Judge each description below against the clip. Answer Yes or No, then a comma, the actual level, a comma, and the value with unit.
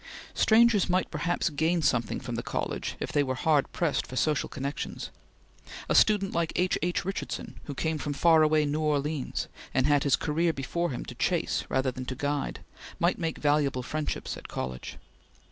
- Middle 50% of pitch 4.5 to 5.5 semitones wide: No, average, 3.4 semitones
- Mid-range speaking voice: Yes, medium, 150 Hz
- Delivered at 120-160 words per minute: No, average, 180 wpm